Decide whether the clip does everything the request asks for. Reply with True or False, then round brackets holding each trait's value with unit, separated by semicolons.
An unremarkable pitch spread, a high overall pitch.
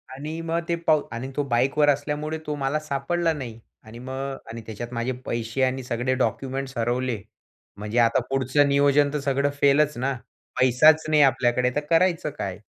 False (3.3 semitones; 135 Hz)